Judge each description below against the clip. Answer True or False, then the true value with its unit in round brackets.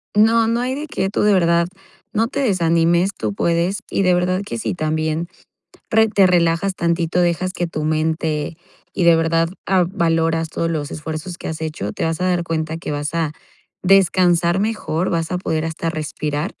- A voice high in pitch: False (170 Hz)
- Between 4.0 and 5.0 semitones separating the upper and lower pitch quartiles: False (2.5 semitones)